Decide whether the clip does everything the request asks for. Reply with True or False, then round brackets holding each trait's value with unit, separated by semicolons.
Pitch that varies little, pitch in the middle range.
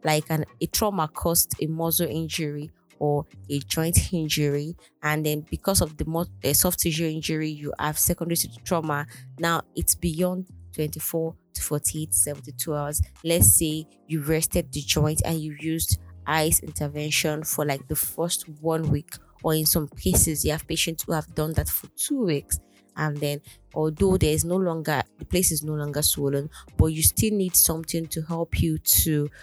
True (2.1 semitones; 155 Hz)